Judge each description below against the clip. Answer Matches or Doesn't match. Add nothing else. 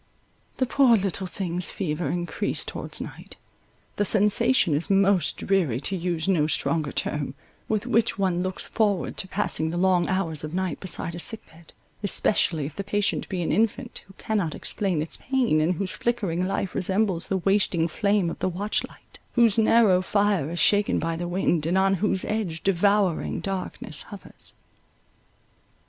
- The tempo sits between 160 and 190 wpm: Matches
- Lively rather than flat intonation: Doesn't match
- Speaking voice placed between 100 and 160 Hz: Doesn't match